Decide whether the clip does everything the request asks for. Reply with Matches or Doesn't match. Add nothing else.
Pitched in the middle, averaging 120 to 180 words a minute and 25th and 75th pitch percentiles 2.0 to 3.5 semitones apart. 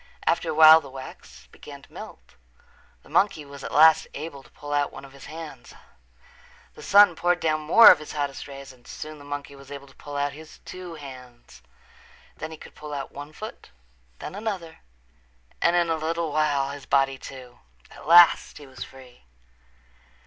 Doesn't match